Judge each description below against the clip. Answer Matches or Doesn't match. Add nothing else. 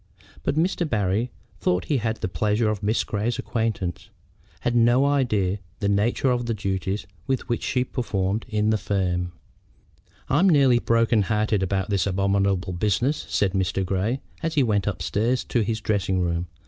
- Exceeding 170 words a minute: Doesn't match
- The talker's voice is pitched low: Matches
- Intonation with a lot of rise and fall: Doesn't match